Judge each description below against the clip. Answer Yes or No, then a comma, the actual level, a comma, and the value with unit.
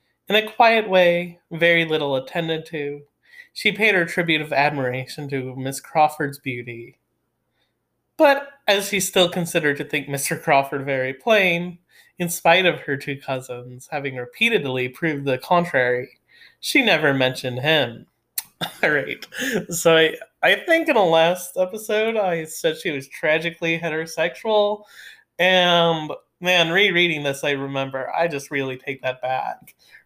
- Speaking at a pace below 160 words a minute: Yes, average, 145 wpm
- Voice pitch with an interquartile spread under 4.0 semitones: No, average, 4.6 semitones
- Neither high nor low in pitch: Yes, medium, 160 Hz